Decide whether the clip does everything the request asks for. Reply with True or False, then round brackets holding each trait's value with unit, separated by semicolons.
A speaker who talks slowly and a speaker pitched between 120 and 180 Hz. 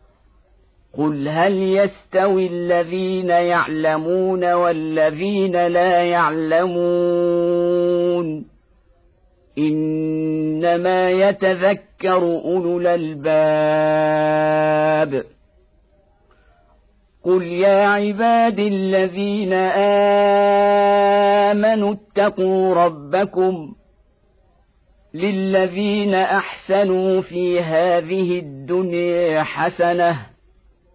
True (50 wpm; 175 Hz)